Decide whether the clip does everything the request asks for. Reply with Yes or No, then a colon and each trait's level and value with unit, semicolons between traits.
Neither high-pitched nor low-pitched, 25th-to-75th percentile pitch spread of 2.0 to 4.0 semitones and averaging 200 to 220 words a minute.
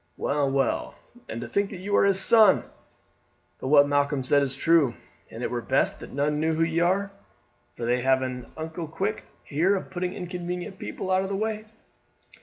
No: medium, 165 Hz; average, 5.2 semitones; fast, 205 wpm